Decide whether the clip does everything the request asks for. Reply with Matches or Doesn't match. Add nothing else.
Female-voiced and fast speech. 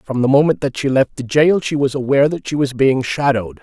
Doesn't match